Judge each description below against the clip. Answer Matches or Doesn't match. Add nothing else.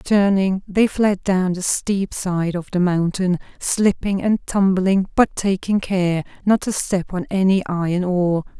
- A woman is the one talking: Matches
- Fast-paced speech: Doesn't match